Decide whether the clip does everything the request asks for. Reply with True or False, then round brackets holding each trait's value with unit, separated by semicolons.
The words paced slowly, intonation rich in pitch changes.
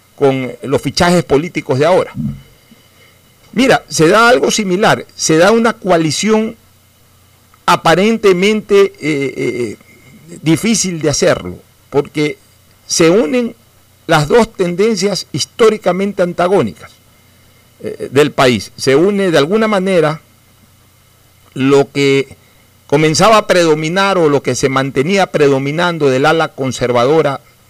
True (110 wpm; 7.8 semitones)